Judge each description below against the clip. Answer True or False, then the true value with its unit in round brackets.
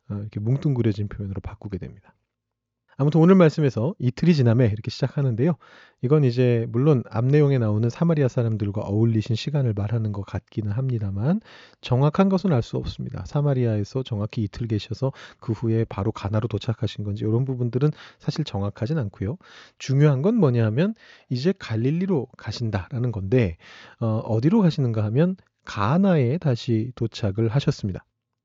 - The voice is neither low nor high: False (120 Hz)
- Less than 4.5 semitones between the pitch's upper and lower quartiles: False (4.8 semitones)